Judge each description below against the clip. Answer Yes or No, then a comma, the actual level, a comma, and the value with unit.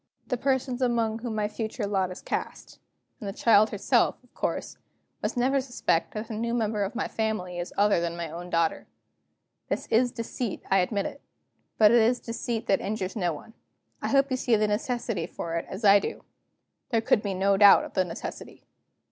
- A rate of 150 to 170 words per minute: No, average, 200 wpm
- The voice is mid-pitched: No, high, 215 Hz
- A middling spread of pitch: Yes, average, 3.5 semitones